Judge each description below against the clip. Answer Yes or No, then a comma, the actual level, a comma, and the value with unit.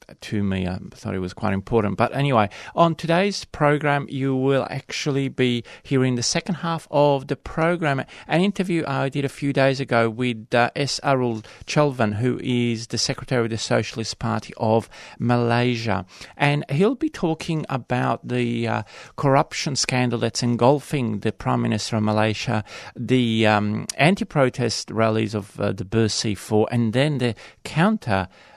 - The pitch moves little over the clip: No, average, 4.1 semitones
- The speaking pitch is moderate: No, low, 125 Hz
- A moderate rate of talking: Yes, average, 155 wpm